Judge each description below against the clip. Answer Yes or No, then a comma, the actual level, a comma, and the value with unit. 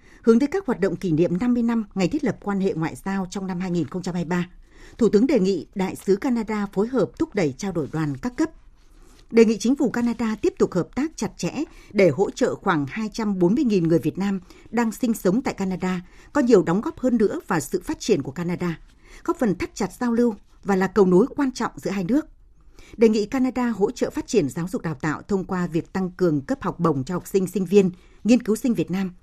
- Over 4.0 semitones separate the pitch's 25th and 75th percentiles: Yes, average, 5.2 semitones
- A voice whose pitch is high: Yes, high, 205 Hz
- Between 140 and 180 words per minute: No, average, 235 wpm